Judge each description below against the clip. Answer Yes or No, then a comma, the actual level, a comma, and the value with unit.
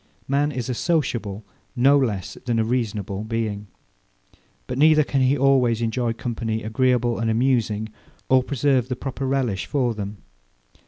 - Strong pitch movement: No, average, 3.2 semitones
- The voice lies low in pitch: Yes, low, 120 Hz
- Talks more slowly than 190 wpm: Yes, average, 150 wpm